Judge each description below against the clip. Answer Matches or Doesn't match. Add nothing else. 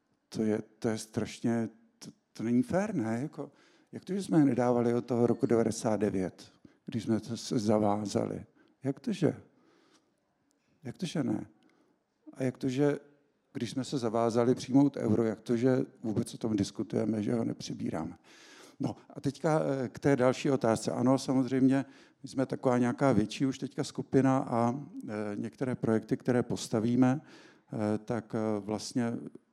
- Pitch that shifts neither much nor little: Matches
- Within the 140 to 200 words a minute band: Matches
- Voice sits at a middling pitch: Doesn't match